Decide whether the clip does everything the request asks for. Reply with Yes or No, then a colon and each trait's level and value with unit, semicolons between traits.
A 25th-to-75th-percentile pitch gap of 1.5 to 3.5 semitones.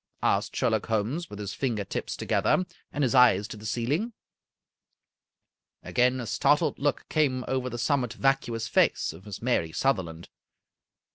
No: average, 4.3 semitones